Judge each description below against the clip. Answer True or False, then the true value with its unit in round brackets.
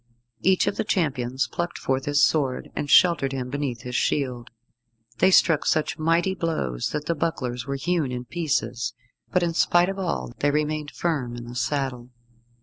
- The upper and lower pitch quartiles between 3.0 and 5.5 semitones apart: True (4.9 semitones)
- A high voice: False (145 Hz)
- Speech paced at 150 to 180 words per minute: True (175 wpm)